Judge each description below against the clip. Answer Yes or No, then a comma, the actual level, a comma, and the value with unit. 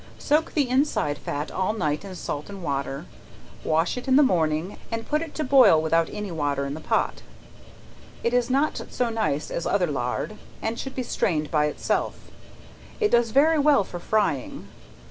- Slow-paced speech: No, average, 185 wpm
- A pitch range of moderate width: No, wide, 8.9 semitones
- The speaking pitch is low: No, high, 200 Hz